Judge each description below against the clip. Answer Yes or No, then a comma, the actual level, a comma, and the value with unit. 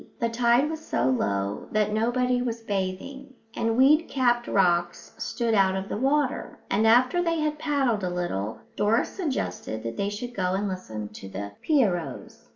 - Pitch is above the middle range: Yes, high, 225 Hz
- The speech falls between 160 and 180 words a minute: Yes, average, 170 wpm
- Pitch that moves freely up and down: Yes, wide, 6.1 semitones